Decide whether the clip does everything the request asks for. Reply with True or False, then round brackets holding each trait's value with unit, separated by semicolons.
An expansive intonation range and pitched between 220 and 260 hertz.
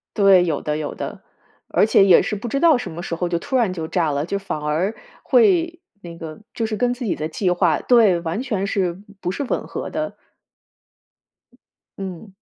False (5.7 semitones; 190 Hz)